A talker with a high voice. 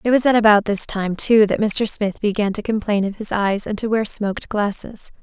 Yes: high, 210 Hz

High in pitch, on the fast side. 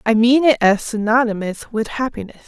No: high, 225 Hz; average, 170 wpm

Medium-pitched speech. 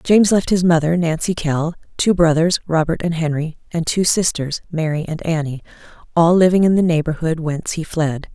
Yes: medium, 165 Hz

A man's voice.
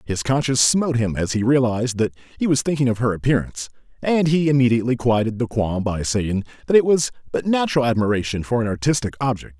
Yes: male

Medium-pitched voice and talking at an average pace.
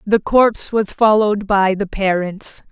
No: high, 205 Hz; average, 155 wpm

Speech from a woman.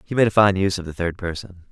No: male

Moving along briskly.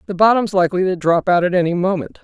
Yes: fast, 240 wpm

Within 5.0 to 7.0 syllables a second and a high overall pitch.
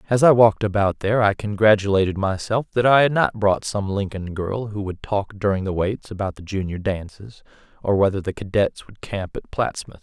No: 5.4 syllables/s; low, 100 Hz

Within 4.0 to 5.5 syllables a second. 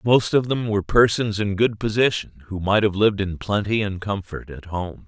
Yes: 5.0 syllables/s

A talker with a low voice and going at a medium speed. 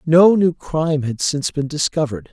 No: medium, 150 Hz; average, 180 wpm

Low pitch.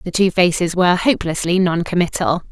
No: medium, 180 Hz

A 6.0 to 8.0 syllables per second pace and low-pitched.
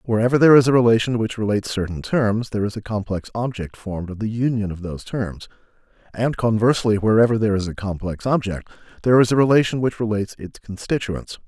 Yes: 6.5 syllables/s; low, 110 Hz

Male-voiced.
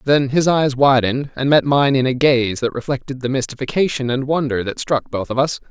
Yes: male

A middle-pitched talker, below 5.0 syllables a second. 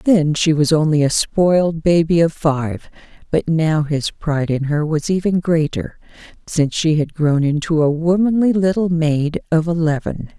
Yes: medium, 160 Hz; 4.5 syllables/s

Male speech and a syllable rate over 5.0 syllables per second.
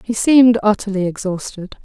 No: female; 5.5 syllables/s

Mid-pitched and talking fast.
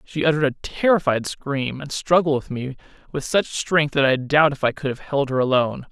Yes: medium, 145 Hz; fast, 225 wpm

